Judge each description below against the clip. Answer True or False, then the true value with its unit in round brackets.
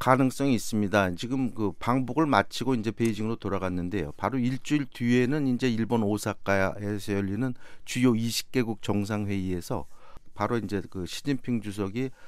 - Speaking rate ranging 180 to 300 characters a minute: False (345 characters per minute)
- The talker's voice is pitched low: True (115 Hz)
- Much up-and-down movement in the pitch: False (4.0 semitones)